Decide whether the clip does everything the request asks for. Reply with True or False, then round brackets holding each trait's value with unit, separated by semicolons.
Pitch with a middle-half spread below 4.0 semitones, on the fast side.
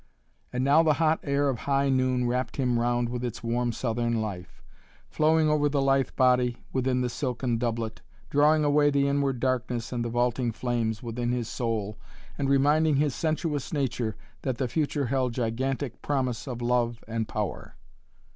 False (2.9 semitones; 170 wpm)